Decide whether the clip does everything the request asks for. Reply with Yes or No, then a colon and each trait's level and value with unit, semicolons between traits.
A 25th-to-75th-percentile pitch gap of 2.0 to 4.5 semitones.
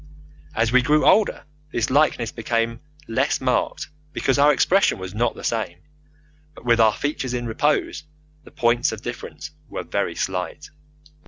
Yes: average, 4.1 semitones